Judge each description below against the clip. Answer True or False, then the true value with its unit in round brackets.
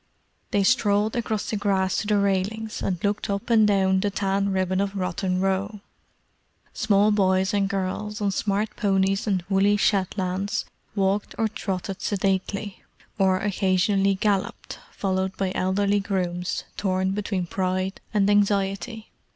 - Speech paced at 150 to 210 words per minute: False (140 wpm)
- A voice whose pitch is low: False (195 Hz)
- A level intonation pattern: True (1.4 semitones)